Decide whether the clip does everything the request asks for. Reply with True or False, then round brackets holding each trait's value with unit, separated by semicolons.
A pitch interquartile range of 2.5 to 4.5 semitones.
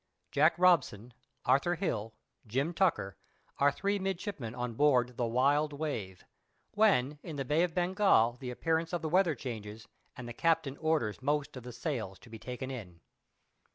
False (5.6 semitones)